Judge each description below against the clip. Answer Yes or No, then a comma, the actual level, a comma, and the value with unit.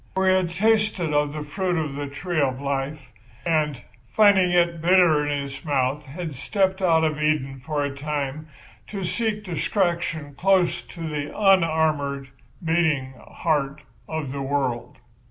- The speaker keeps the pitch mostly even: No, average, 3.9 semitones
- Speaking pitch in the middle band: Yes, medium, 155 Hz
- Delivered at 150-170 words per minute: Yes, average, 155 wpm